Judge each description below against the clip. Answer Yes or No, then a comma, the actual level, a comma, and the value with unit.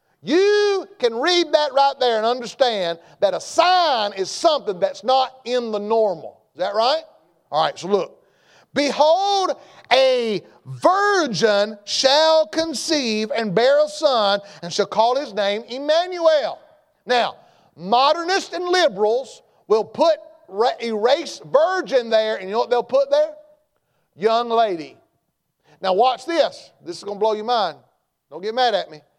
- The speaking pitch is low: No, very high, 265 Hz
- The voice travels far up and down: Yes, wide, 6.5 semitones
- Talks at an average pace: Yes, average, 150 wpm